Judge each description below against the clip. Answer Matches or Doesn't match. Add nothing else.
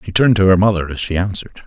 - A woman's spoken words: Doesn't match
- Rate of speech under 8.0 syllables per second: Doesn't match